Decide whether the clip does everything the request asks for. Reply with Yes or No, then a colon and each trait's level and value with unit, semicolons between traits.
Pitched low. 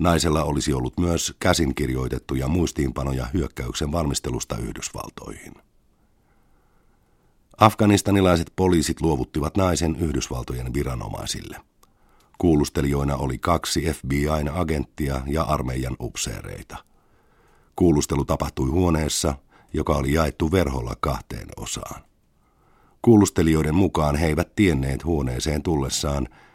Yes: very low, 75 Hz